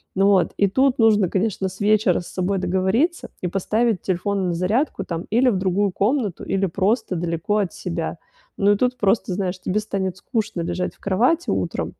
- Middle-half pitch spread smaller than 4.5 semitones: Yes, average, 2.8 semitones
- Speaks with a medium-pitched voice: No, high, 195 Hz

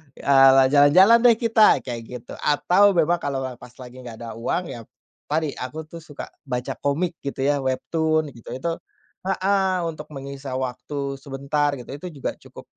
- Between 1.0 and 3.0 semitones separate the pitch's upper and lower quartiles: No, average, 4.0 semitones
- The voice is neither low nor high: Yes, medium, 145 Hz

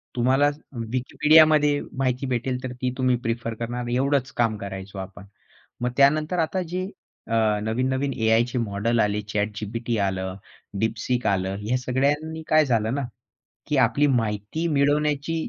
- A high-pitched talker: No, low, 125 Hz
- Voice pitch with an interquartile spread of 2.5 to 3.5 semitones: No, average, 4.3 semitones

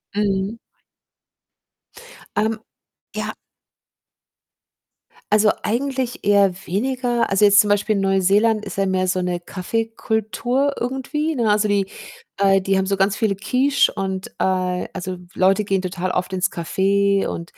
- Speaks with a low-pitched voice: No, high, 200 Hz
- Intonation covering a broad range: No, average, 2.8 semitones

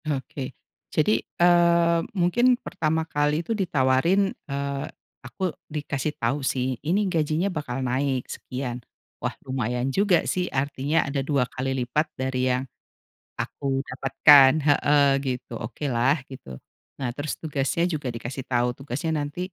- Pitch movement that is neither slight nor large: Yes, average, 3.5 semitones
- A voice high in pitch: No, medium, 140 Hz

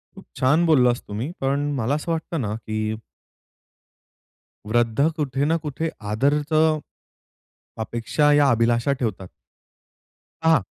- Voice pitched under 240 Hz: Yes, low, 135 Hz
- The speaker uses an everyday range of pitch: Yes, average, 4.6 semitones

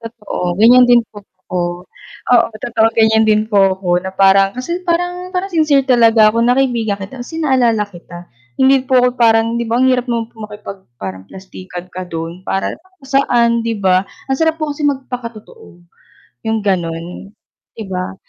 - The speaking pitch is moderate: No, high, 225 Hz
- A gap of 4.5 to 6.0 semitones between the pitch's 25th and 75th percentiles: Yes, average, 4.9 semitones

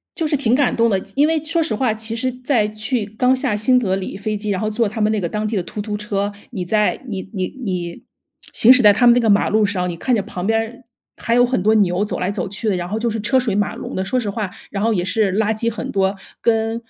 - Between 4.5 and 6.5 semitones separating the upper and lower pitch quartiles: No, average, 2.9 semitones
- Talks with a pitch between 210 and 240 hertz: Yes, high, 215 Hz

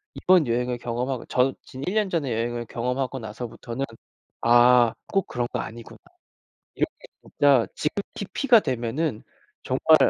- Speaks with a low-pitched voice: Yes, low, 125 Hz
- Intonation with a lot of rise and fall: No, average, 3.4 semitones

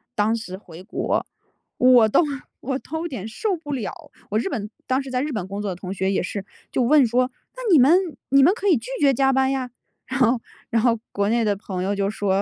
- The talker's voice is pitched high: Yes, high, 235 Hz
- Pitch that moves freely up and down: No, average, 4.8 semitones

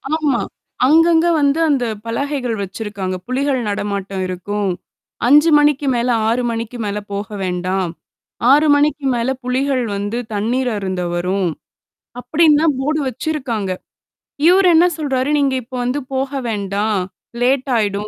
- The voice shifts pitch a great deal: Yes, wide, 5.8 semitones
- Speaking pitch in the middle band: No, very high, 250 Hz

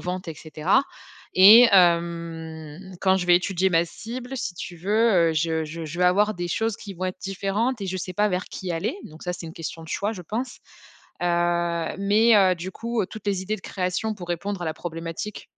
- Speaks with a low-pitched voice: No, medium, 180 Hz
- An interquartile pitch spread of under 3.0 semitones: No, average, 3.3 semitones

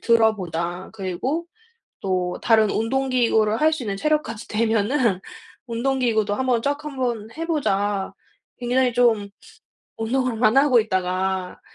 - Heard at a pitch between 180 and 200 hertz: No, high, 225 Hz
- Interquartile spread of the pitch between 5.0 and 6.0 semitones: No, average, 4.4 semitones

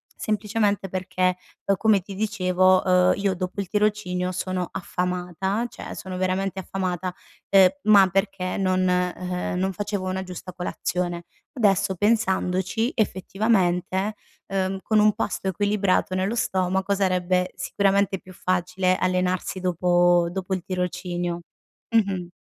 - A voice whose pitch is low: No, medium, 185 Hz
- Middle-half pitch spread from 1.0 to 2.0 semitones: Yes, narrow, 1.6 semitones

